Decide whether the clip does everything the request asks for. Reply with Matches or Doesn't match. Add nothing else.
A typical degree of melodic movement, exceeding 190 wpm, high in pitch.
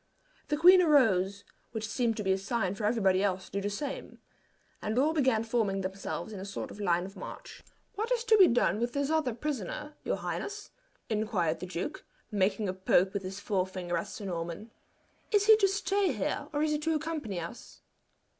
Doesn't match